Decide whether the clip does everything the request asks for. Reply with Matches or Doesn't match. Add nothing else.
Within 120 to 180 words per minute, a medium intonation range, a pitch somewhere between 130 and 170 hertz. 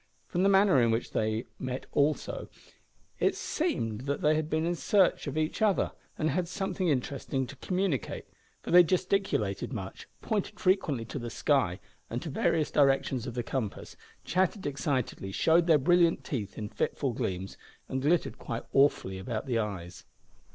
Doesn't match